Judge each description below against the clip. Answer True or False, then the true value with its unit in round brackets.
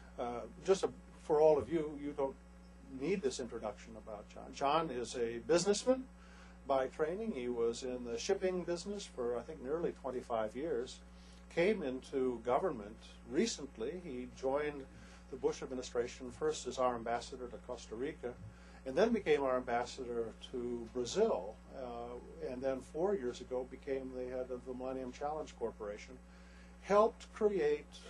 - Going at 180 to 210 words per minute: False (150 wpm)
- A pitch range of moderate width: True (4.7 semitones)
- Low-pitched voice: True (125 Hz)